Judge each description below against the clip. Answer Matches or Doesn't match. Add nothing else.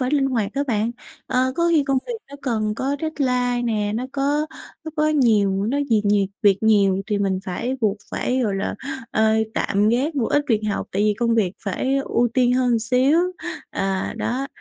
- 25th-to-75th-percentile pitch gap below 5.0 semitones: Matches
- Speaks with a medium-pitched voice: Doesn't match